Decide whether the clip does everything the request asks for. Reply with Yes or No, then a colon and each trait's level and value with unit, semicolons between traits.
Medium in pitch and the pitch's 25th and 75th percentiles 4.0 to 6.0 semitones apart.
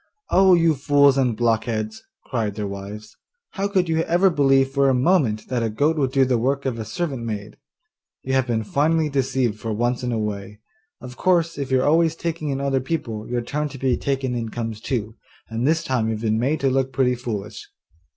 No: low, 130 Hz; average, 4.3 semitones